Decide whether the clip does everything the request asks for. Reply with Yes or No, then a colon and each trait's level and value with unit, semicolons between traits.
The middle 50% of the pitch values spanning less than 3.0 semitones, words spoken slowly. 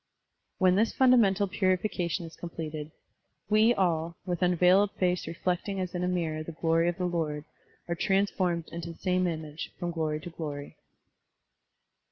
No: narrow, 2.4 semitones; average, 160 wpm